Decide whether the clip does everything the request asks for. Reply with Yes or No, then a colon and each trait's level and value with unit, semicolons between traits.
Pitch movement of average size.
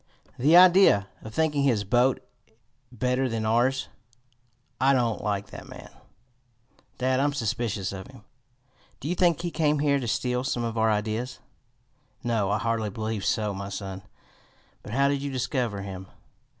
Yes: average, 4.5 semitones